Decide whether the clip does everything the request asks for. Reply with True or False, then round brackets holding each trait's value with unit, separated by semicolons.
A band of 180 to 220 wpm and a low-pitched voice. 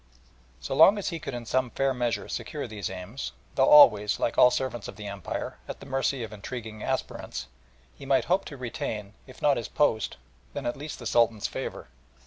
True (195 wpm; 120 Hz)